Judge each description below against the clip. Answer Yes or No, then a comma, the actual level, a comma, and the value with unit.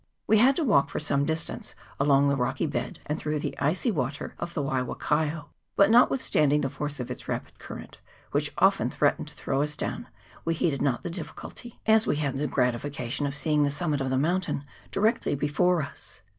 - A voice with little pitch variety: No, average, 3.5 semitones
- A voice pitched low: No, medium, 150 Hz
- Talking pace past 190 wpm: Yes, average, 200 wpm